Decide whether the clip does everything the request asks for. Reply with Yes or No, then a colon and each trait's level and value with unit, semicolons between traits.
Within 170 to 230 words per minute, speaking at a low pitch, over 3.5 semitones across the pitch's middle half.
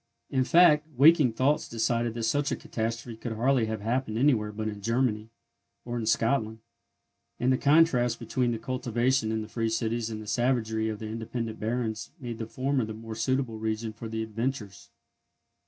No: average, 180 wpm; low, 115 Hz; narrow, 2.5 semitones